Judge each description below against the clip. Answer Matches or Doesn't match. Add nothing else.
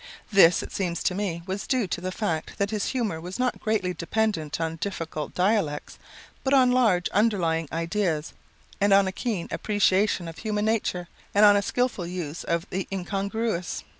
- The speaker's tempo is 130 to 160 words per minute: Doesn't match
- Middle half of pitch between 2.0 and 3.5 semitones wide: Doesn't match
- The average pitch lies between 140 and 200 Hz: Matches